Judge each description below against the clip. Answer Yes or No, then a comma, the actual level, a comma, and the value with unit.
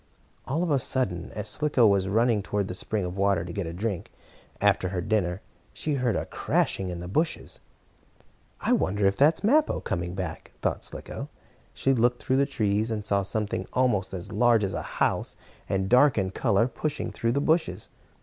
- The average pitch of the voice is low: Yes, low, 105 Hz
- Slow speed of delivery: No, average, 195 wpm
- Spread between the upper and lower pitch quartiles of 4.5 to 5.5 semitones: Yes, average, 4.9 semitones